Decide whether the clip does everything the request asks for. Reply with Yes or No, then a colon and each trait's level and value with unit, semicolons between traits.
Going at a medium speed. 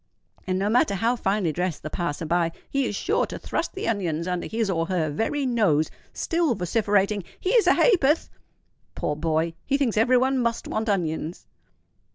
Yes: average, 180 wpm